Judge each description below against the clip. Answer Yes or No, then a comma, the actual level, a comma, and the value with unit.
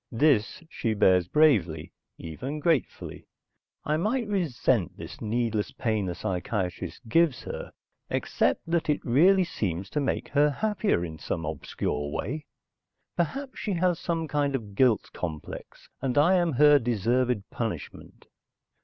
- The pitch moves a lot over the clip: Yes, wide, 7.9 semitones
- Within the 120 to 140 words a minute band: Yes, slow, 135 wpm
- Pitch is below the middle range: Yes, low, 125 Hz